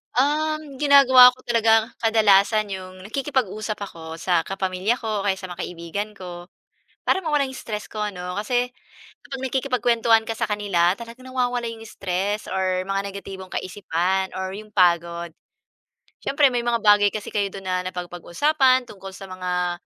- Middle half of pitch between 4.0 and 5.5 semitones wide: Yes, average, 4.6 semitones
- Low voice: No, high, 205 Hz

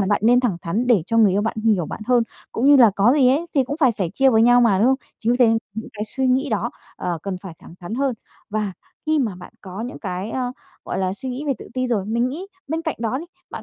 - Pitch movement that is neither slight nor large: Yes, average, 4.1 semitones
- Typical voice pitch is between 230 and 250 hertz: Yes, high, 235 Hz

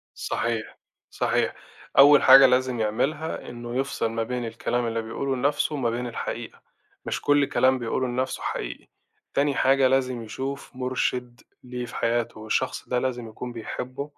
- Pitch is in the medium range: No, low, 125 Hz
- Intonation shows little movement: Yes, narrow, 2.2 semitones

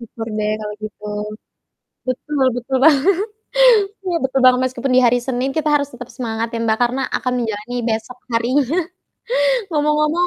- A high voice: Yes, very high, 250 Hz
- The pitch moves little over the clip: No, average, 3.2 semitones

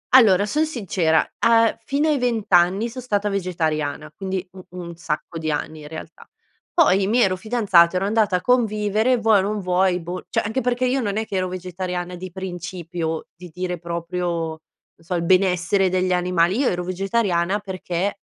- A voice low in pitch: No, medium, 185 Hz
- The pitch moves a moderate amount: Yes, average, 3.3 semitones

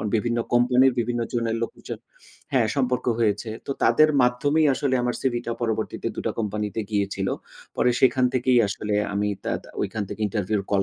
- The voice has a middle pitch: No, low, 120 Hz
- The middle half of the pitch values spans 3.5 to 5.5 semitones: No, average, 3.1 semitones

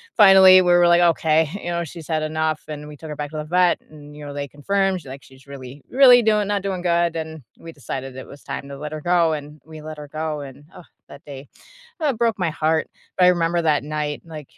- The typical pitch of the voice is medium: Yes, medium, 155 Hz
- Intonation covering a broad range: No, average, 3.1 semitones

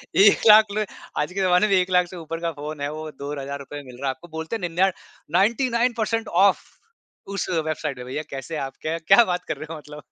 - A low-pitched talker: No, medium, 170 Hz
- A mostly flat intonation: No, average, 4.9 semitones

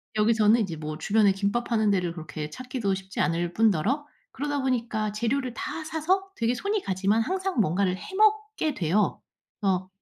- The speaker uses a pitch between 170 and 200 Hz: No, high, 220 Hz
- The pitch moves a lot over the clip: Yes, wide, 6.1 semitones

